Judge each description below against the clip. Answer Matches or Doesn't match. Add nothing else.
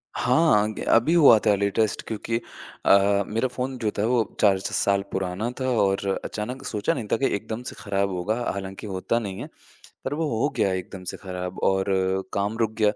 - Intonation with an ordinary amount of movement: Matches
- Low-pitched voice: Matches